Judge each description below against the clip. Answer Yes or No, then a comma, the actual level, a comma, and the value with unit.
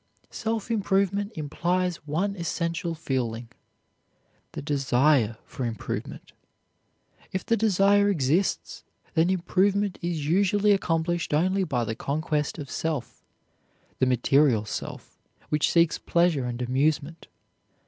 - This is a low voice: No, medium, 165 Hz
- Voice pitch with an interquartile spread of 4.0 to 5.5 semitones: Yes, average, 5.2 semitones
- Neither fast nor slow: No, slow, 110 wpm